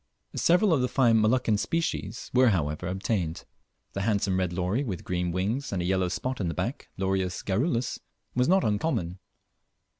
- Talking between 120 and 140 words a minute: No, average, 170 wpm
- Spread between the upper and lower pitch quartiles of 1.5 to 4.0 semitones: No, wide, 5.6 semitones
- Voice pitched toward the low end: Yes, low, 100 Hz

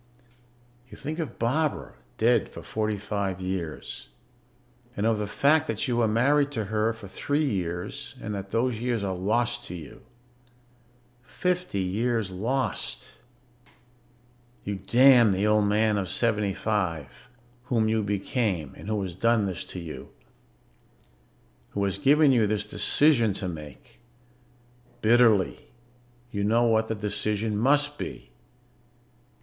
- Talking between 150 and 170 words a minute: No, slow, 135 wpm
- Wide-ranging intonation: No, average, 3.5 semitones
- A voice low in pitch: Yes, low, 110 Hz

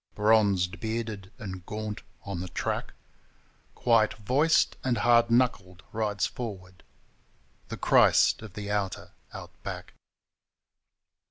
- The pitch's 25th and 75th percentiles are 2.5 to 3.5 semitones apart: Yes, average, 3.2 semitones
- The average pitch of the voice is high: No, low, 105 Hz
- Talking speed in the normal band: No, slow, 110 wpm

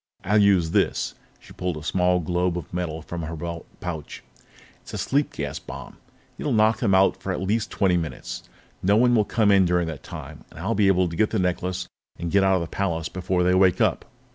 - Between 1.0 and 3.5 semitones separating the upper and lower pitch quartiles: Yes, average, 2.7 semitones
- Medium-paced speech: No, fast, 230 wpm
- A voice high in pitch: No, very low, 90 Hz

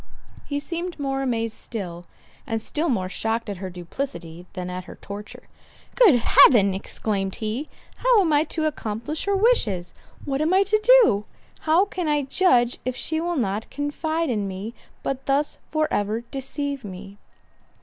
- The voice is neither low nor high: No, very high, 255 Hz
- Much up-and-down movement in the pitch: Yes, wide, 7.5 semitones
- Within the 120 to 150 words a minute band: No, average, 160 wpm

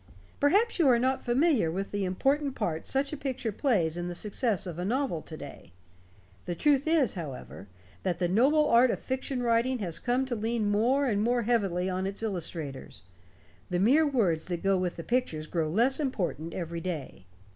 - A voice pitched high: Yes, high, 215 Hz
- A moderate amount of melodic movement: No, wide, 6.9 semitones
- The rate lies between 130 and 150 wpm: No, average, 190 wpm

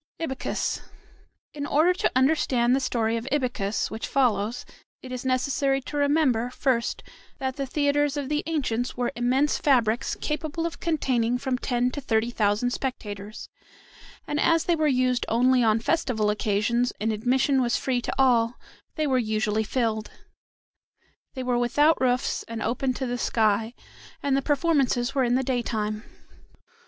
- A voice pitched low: No, very high, 250 Hz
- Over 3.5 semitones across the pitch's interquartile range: No, average, 3.2 semitones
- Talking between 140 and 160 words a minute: Yes, average, 155 wpm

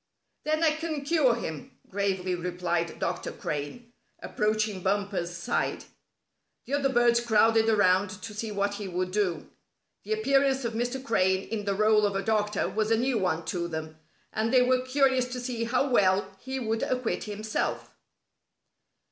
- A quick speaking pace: No, average, 165 wpm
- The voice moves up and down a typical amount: Yes, average, 4.7 semitones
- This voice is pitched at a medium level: No, high, 215 Hz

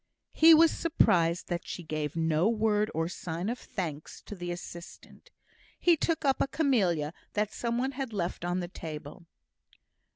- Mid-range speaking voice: Yes, medium, 180 Hz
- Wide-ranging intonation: Yes, wide, 6.6 semitones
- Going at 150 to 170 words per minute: Yes, average, 165 wpm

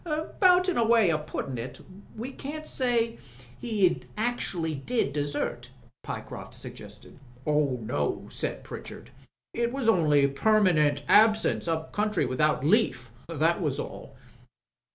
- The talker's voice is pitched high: No, medium, 175 Hz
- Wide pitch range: Yes, wide, 8.1 semitones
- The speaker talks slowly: Yes, slow, 130 wpm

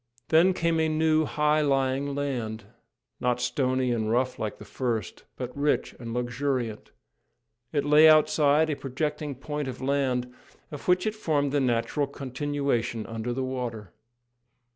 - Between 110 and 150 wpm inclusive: Yes, average, 145 wpm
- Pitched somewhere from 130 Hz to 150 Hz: Yes, low, 135 Hz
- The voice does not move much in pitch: No, average, 3.4 semitones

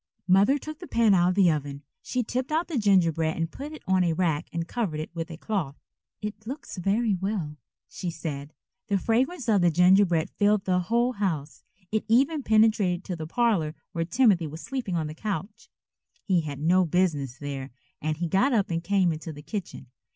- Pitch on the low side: No, medium, 185 Hz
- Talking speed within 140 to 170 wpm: No, average, 200 wpm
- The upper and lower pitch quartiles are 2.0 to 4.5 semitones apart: No, average, 5.2 semitones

